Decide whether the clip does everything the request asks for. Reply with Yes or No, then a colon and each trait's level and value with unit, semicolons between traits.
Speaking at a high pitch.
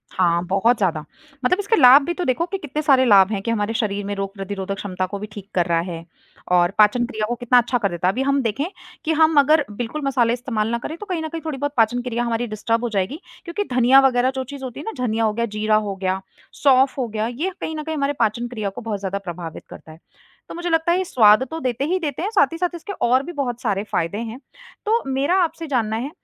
Yes: high, 240 Hz